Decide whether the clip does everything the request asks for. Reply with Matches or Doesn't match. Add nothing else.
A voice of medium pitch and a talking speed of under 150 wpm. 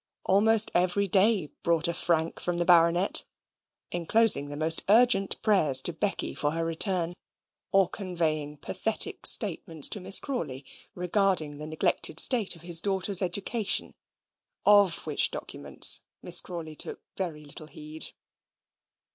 Matches